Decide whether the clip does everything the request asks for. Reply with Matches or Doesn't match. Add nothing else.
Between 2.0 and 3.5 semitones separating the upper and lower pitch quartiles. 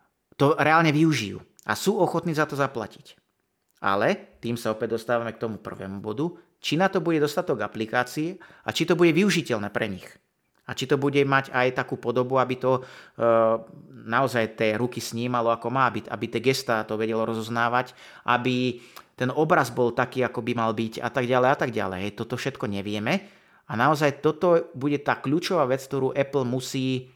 Doesn't match